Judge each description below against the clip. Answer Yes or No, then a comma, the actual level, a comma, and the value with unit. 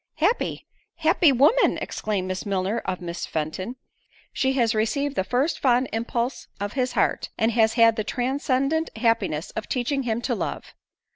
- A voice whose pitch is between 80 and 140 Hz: No, high, 235 Hz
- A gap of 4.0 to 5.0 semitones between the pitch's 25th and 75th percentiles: Yes, average, 4.4 semitones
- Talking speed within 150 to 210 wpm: Yes, average, 160 wpm